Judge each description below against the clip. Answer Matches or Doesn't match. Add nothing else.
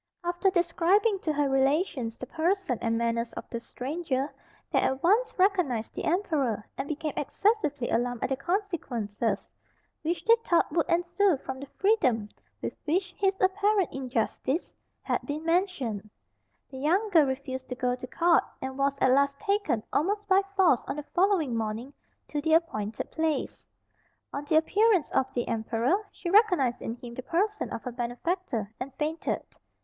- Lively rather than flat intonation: Matches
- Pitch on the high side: Matches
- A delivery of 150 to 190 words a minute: Matches